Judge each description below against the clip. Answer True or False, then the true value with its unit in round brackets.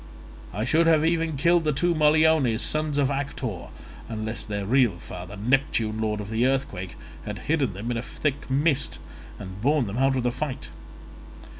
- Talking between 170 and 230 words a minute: True (175 wpm)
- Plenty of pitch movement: True (5.8 semitones)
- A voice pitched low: True (130 Hz)